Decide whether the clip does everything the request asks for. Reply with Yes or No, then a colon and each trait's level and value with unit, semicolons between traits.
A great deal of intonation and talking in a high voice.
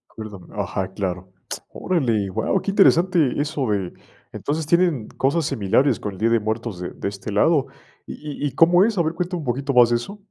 No: wide, 7.8 semitones; low, 135 Hz